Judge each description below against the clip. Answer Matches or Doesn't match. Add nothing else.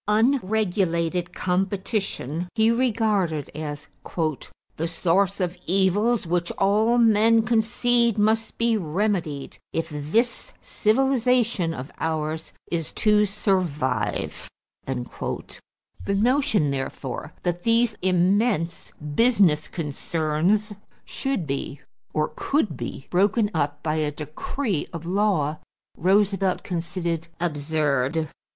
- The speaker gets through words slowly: Matches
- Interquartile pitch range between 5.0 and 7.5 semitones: Matches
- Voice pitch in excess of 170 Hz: Matches